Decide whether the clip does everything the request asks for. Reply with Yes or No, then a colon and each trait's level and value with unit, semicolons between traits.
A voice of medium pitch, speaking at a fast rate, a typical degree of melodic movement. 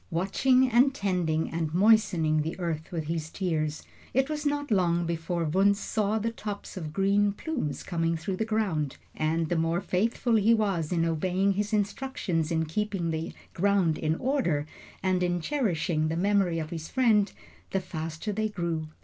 No: medium, 180 Hz; average, 170 wpm; average, 4.4 semitones